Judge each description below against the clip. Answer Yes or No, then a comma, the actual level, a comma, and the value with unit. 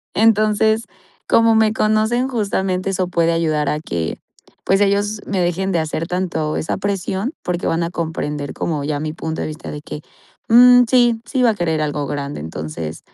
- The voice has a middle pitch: Yes, medium, 180 Hz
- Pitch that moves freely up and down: Yes, wide, 5.8 semitones